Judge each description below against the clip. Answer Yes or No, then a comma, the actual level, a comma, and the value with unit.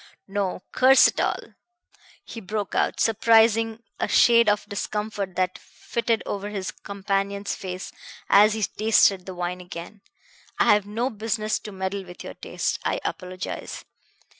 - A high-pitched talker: Yes, high, 205 Hz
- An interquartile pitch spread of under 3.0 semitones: Yes, narrow, 2.6 semitones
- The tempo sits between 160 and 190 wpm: No, average, 145 wpm